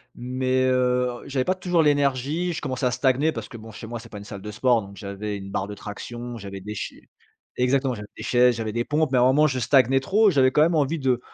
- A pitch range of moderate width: Yes, average, 3.9 semitones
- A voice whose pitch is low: Yes, low, 125 Hz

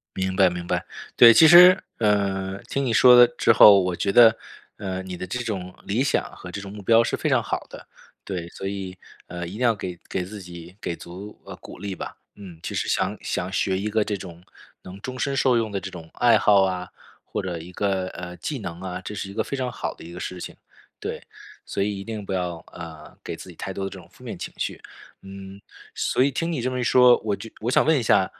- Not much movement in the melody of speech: No, average, 3.8 semitones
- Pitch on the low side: Yes, low, 100 Hz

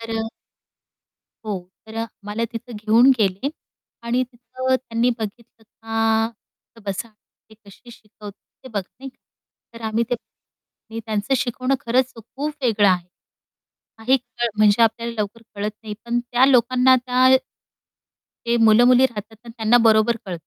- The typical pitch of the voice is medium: No, high, 230 Hz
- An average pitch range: No, narrow, 2.2 semitones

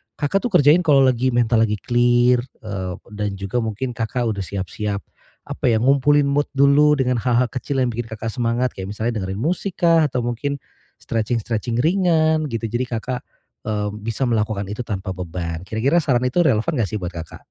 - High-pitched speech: No, low, 120 Hz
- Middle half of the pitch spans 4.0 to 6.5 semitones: Yes, average, 4.4 semitones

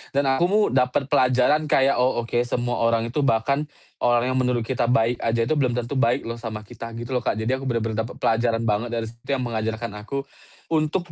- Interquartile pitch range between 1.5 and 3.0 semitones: Yes, narrow, 2.5 semitones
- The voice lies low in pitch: Yes, low, 120 Hz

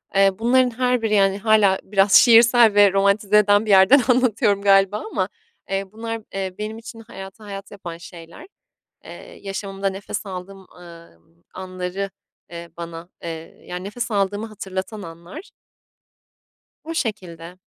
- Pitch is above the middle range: Yes, high, 195 Hz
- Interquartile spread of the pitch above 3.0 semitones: No, narrow, 2.6 semitones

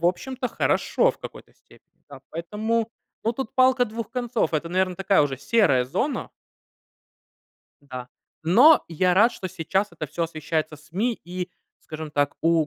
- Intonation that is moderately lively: No, wide, 6.7 semitones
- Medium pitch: Yes, medium, 180 Hz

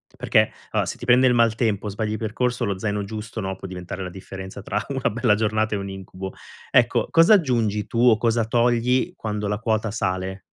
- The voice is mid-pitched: No, low, 110 Hz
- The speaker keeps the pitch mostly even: No, average, 3.0 semitones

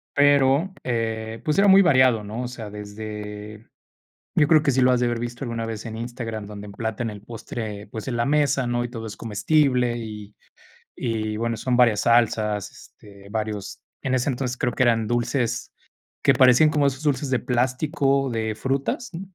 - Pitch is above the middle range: No, low, 120 Hz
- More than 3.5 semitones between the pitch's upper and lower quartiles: No, average, 3.2 semitones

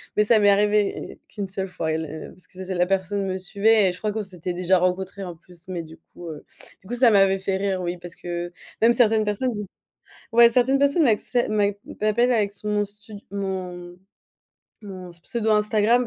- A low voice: No, high, 195 Hz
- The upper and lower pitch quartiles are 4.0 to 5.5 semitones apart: No, average, 2.9 semitones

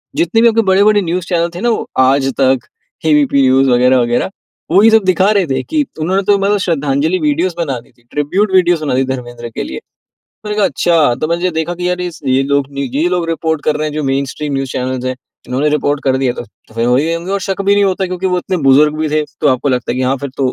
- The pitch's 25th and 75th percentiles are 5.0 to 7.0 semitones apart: Yes, wide, 5.6 semitones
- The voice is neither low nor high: Yes, medium, 155 Hz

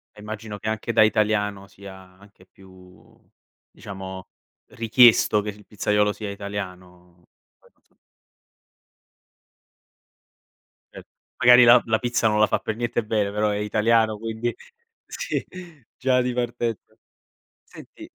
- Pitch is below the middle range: Yes, low, 105 Hz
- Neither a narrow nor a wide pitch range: No, narrow, 2.3 semitones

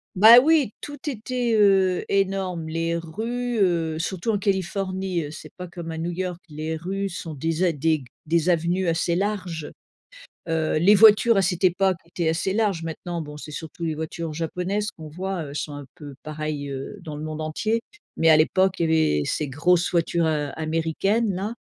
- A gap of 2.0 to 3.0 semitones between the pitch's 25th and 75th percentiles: No, average, 3.5 semitones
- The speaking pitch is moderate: Yes, medium, 170 Hz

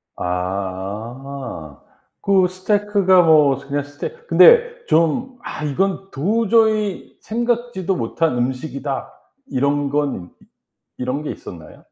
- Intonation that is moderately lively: No, wide, 7.5 semitones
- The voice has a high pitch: No, medium, 150 Hz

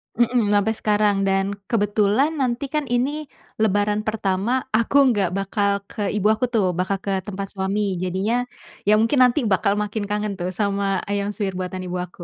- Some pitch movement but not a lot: No, narrow, 2.1 semitones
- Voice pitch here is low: No, high, 205 Hz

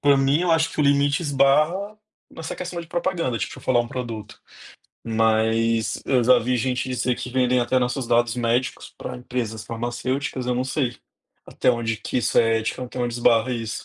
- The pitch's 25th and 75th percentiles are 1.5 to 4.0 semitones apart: Yes, average, 2.9 semitones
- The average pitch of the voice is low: Yes, low, 125 Hz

